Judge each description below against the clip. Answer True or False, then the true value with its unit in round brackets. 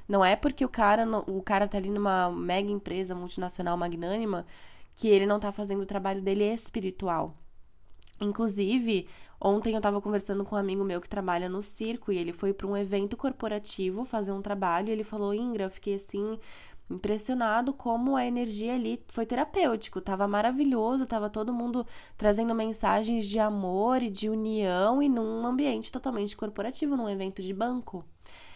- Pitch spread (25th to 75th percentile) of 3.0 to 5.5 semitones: False (2.6 semitones)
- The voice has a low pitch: False (205 Hz)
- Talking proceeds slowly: False (170 wpm)